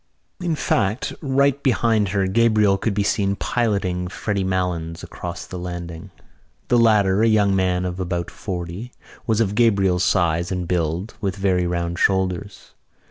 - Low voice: Yes, very low, 95 Hz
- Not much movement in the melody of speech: No, average, 3.3 semitones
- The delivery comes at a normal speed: Yes, average, 150 wpm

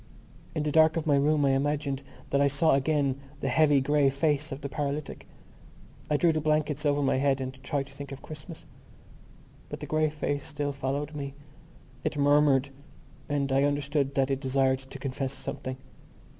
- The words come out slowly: No, average, 185 wpm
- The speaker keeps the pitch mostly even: Yes, narrow, 1.5 semitones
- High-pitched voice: No, medium, 140 Hz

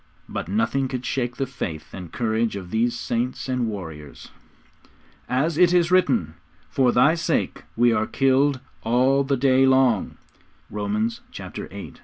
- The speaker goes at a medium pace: Yes, average, 145 wpm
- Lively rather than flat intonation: No, average, 3.7 semitones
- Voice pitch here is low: Yes, low, 125 Hz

